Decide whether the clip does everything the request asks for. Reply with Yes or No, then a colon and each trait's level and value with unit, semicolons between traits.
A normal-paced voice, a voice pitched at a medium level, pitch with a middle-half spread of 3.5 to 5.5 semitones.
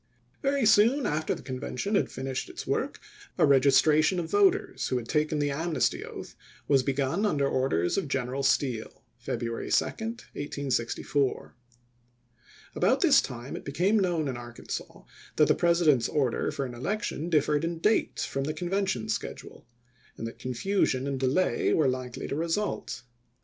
Yes: average, 160 wpm; medium, 145 Hz; average, 5.2 semitones